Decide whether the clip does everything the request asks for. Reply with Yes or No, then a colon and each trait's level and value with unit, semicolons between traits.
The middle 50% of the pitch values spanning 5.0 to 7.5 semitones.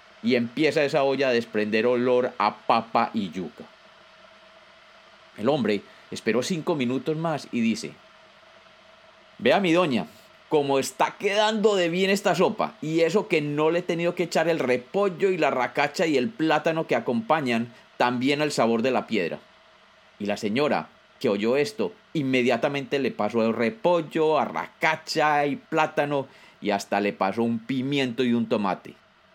Yes: average, 5.3 semitones